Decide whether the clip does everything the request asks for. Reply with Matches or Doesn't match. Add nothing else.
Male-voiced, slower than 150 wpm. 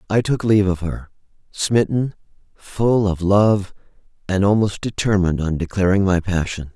Matches